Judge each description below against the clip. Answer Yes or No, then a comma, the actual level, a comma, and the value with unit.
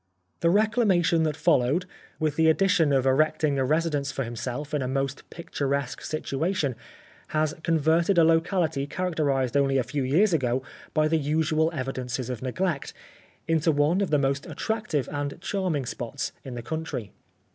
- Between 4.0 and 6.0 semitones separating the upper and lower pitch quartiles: No, average, 3.4 semitones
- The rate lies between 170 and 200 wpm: No, average, 160 wpm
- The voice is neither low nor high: Yes, medium, 150 Hz